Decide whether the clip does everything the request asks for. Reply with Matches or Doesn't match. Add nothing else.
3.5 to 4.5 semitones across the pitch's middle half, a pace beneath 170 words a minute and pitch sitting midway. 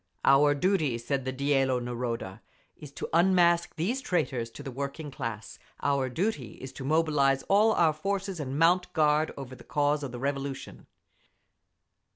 Matches